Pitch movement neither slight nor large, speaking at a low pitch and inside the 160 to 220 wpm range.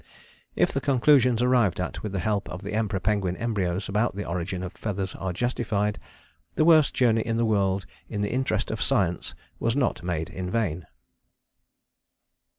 Yes: average, 3.9 semitones; low, 105 Hz; average, 170 wpm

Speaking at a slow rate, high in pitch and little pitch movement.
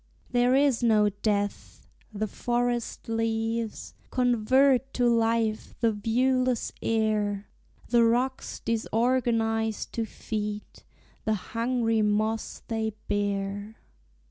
Yes: slow, 95 wpm; high, 225 Hz; narrow, 2.2 semitones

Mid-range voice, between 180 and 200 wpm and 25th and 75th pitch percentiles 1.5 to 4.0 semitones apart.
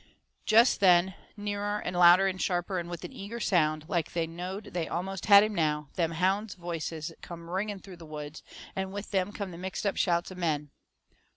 Yes: medium, 180 Hz; average, 195 wpm; average, 2.9 semitones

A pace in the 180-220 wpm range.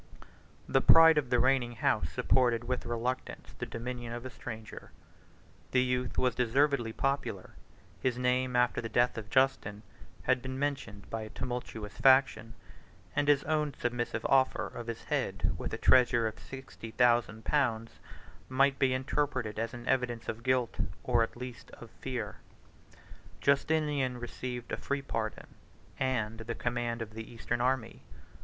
No: average, 155 wpm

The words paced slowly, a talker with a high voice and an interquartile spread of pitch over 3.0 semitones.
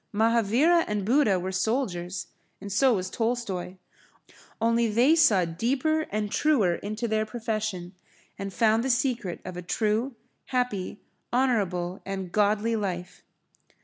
Yes: slow, 130 wpm; high, 215 Hz; average, 4.1 semitones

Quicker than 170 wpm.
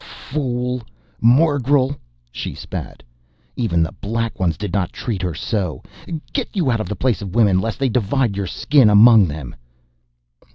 No: average, 160 wpm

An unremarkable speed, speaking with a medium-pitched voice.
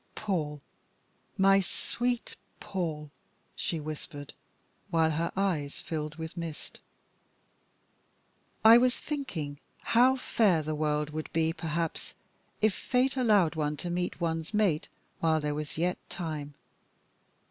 No: slow, 120 wpm; medium, 165 Hz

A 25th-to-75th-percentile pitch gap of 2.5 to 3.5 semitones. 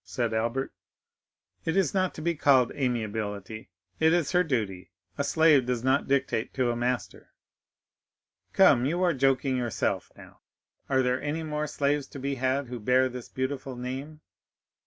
Yes: average, 3.2 semitones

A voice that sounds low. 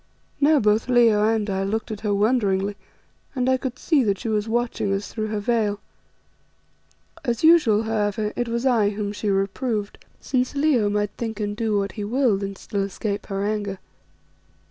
No: high, 215 Hz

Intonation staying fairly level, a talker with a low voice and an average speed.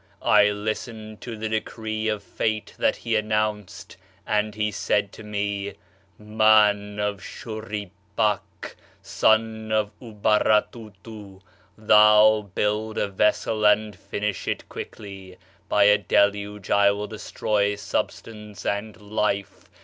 No: narrow, 1.1 semitones; low, 105 Hz; slow, 120 wpm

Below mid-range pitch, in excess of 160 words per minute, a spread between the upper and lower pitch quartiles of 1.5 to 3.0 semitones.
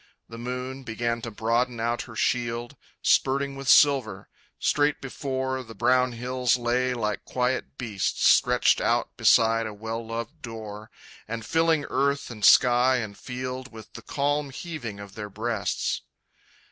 No: low, 120 Hz; average, 145 wpm; narrow, 2.6 semitones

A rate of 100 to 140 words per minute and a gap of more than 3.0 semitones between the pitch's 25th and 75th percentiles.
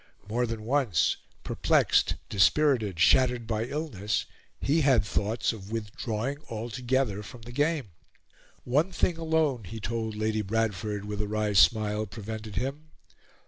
Yes: slow, 135 wpm; average, 3.7 semitones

